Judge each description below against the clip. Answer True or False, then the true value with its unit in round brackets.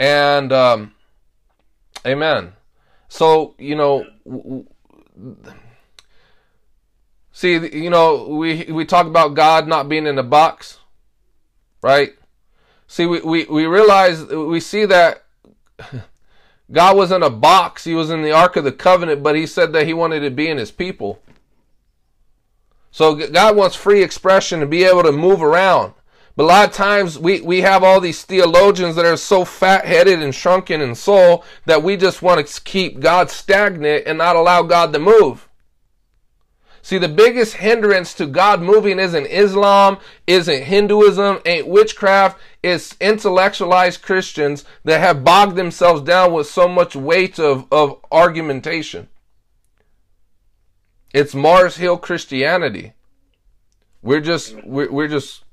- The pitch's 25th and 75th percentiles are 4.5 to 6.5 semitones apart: True (4.8 semitones)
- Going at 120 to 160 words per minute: True (145 wpm)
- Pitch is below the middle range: False (170 Hz)